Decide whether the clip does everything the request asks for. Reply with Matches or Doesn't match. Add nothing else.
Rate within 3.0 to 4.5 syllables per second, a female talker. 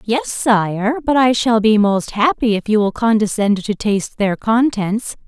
Matches